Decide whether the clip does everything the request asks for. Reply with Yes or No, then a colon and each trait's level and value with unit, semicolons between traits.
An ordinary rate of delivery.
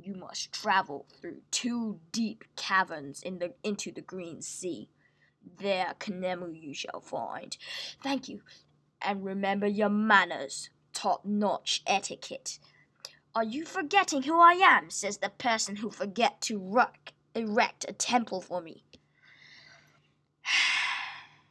No: slow, 125 wpm